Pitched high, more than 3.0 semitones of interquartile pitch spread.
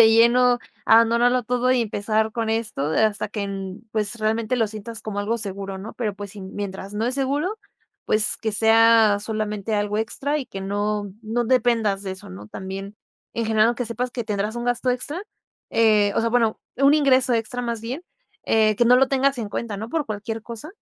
No: high, 225 Hz; average, 2.7 semitones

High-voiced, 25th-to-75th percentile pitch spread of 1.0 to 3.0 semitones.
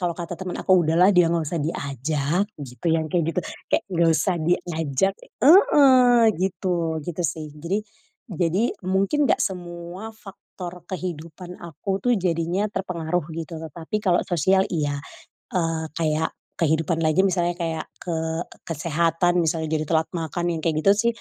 No: medium, 170 Hz; narrow, 2.5 semitones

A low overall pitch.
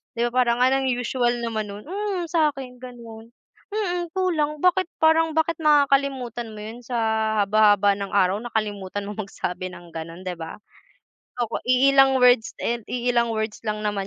No: high, 240 Hz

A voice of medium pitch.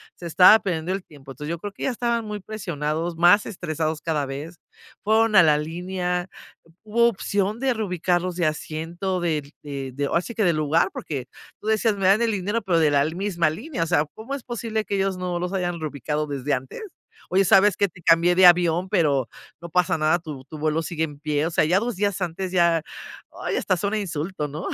Yes: medium, 175 Hz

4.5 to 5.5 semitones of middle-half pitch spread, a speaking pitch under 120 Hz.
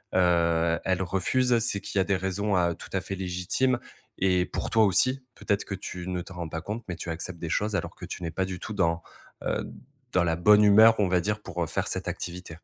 No: average, 3.1 semitones; very low, 95 Hz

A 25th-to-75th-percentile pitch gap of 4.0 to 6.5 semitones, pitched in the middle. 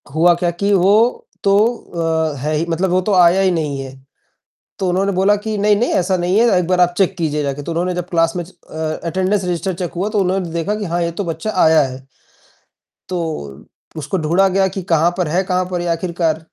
No: average, 2.7 semitones; medium, 175 Hz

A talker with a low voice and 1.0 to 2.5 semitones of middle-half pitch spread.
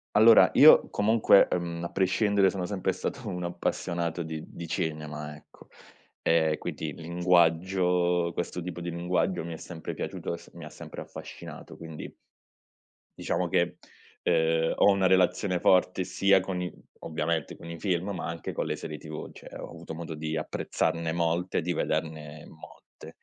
Yes: very low, 85 Hz; narrow, 2.2 semitones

